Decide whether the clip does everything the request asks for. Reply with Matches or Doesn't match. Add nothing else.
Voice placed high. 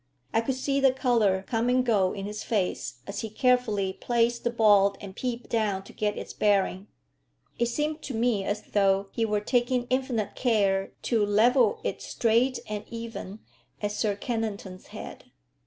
Matches